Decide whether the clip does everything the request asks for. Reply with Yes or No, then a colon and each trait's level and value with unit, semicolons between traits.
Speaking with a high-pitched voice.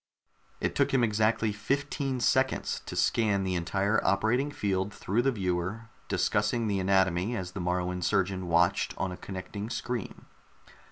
No: low, 100 Hz